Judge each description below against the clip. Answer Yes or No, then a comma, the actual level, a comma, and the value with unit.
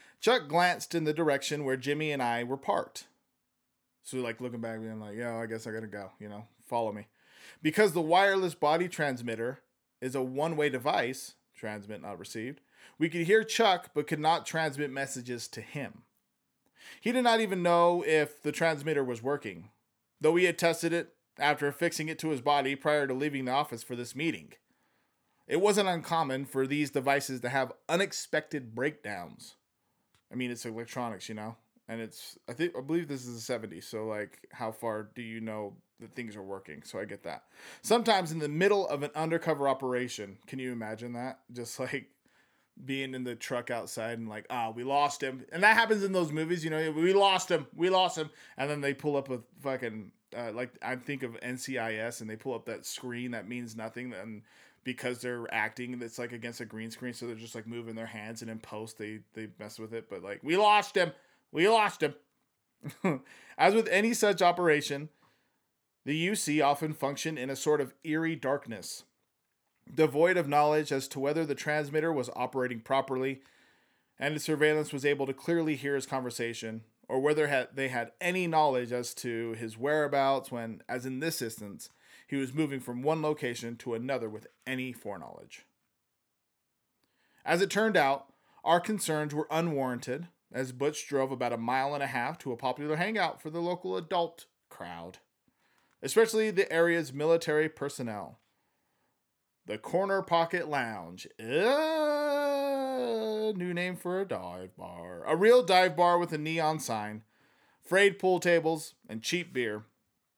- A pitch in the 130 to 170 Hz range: Yes, medium, 140 Hz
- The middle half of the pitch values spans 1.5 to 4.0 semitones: No, average, 5.3 semitones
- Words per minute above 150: Yes, average, 180 wpm